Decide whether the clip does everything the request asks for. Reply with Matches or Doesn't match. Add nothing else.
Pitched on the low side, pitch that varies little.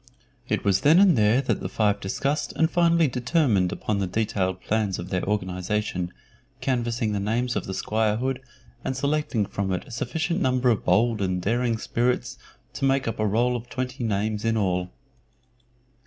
Doesn't match